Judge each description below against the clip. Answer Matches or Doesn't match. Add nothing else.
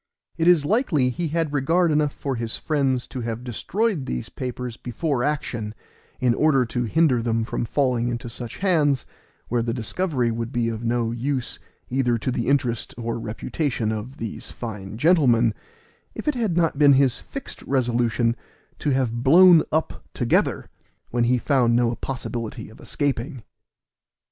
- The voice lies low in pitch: Matches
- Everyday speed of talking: Matches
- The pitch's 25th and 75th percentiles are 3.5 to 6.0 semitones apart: Matches